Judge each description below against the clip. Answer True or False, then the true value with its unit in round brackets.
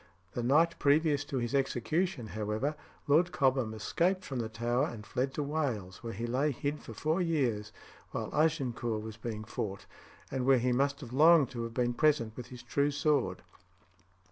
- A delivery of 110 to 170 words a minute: False (180 wpm)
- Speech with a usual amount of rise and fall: True (4.2 semitones)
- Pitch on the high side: False (130 Hz)